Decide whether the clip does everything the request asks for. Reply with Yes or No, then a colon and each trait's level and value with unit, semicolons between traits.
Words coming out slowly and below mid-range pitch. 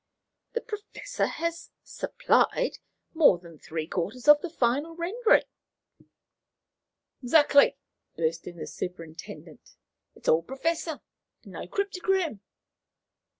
No: slow, 105 wpm; very high, 295 Hz